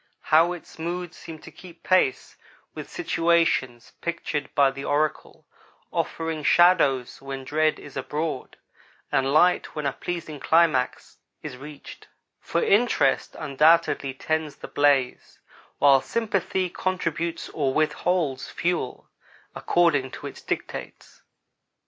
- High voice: No, medium, 155 Hz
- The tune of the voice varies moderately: Yes, average, 3.7 semitones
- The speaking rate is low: Yes, slow, 120 wpm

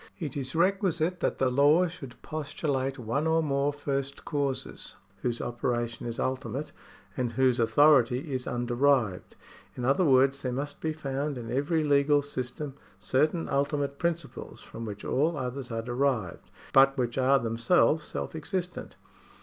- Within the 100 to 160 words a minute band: Yes, average, 150 wpm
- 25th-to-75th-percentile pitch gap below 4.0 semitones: Yes, average, 3.3 semitones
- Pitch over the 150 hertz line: No, medium, 140 Hz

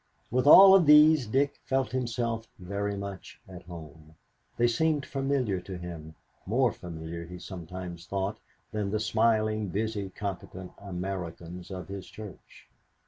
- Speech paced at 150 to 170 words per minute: No, average, 140 wpm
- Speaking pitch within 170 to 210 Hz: No, low, 100 Hz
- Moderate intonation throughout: Yes, average, 4.9 semitones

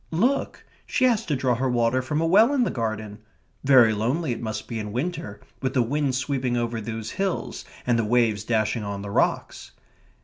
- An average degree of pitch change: Yes, average, 4.7 semitones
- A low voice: Yes, low, 125 Hz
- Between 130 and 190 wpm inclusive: No, average, 200 wpm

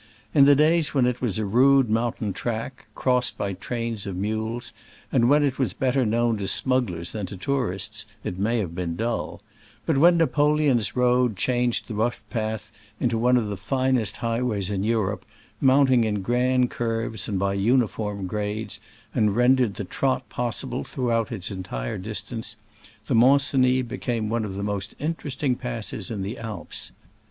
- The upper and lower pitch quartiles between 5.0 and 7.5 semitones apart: No, average, 3.6 semitones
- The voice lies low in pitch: Yes, low, 115 Hz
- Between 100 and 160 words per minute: No, average, 175 wpm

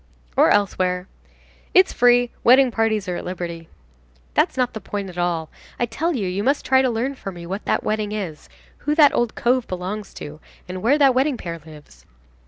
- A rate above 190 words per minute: Yes, average, 200 wpm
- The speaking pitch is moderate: No, high, 210 Hz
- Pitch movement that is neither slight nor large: No, wide, 5.7 semitones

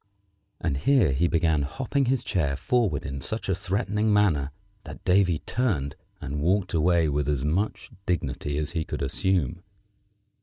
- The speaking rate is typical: Yes, average, 155 wpm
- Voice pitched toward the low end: Yes, very low, 85 Hz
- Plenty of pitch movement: Yes, wide, 6.0 semitones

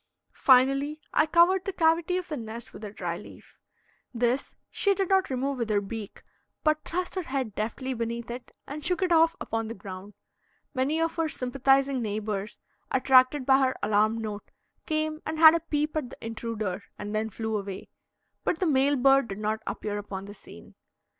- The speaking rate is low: No, average, 185 wpm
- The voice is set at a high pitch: Yes, very high, 255 Hz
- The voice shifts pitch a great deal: Yes, wide, 6.2 semitones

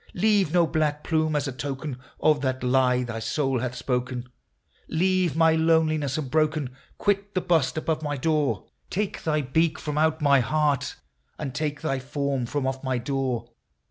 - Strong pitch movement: No, average, 3.3 semitones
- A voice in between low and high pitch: Yes, medium, 145 Hz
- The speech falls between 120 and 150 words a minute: No, average, 175 wpm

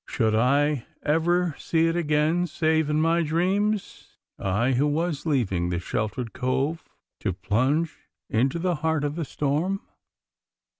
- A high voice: No, medium, 150 Hz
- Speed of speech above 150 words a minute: No, average, 140 wpm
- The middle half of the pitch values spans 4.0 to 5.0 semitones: Yes, average, 4.5 semitones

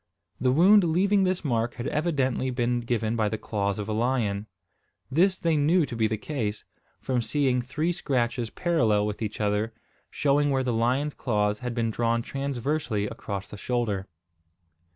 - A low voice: Yes, low, 120 Hz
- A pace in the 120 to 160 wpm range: No, average, 170 wpm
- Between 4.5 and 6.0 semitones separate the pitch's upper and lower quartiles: Yes, average, 4.8 semitones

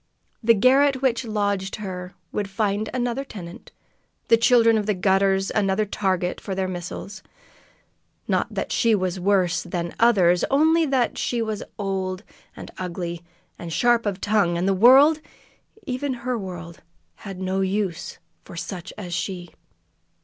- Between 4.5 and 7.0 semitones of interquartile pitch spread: No, average, 4.0 semitones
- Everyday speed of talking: Yes, average, 150 wpm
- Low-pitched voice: No, high, 200 Hz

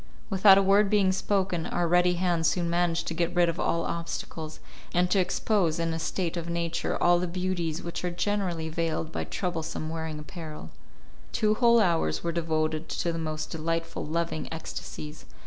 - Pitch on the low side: No, medium, 170 Hz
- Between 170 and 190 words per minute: Yes, average, 180 wpm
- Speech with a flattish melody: Yes, narrow, 1.8 semitones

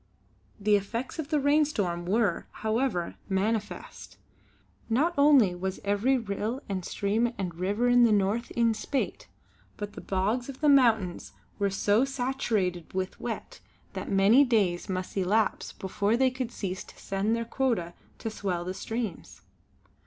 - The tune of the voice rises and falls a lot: No, average, 4.3 semitones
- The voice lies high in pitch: Yes, high, 215 Hz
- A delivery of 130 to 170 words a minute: Yes, average, 150 wpm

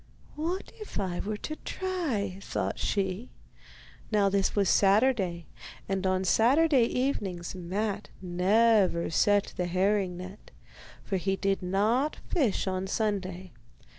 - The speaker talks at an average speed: No, slow, 125 wpm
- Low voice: No, high, 200 Hz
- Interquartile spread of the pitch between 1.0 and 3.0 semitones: No, average, 3.4 semitones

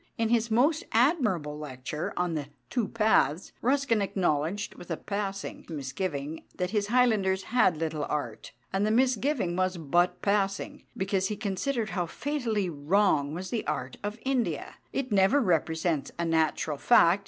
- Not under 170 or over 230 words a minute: No, average, 155 wpm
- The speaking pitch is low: No, high, 195 Hz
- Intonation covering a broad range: Yes, wide, 5.7 semitones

